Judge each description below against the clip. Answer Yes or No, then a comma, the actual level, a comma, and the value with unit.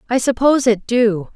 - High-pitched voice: Yes, high, 235 Hz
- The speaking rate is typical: Yes, average, 175 wpm